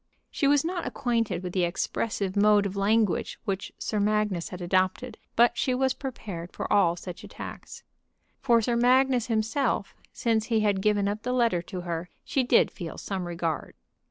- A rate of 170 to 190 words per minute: Yes, average, 175 wpm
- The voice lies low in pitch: No, high, 210 Hz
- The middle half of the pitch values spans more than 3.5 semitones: Yes, average, 4.4 semitones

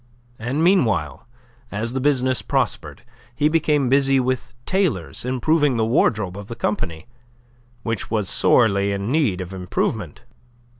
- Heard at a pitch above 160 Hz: No, low, 120 Hz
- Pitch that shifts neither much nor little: No, wide, 5.8 semitones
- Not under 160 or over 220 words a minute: No, slow, 135 wpm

